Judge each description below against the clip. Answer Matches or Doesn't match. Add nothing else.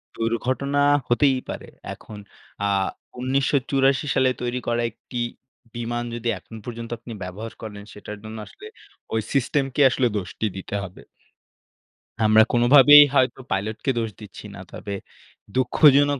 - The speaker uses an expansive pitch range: Doesn't match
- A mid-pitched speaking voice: Doesn't match